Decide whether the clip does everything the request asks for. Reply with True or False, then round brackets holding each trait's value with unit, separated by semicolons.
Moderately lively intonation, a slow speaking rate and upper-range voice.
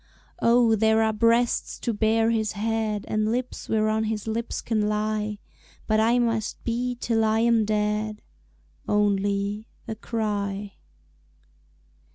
False (1.3 semitones; 130 wpm; 220 Hz)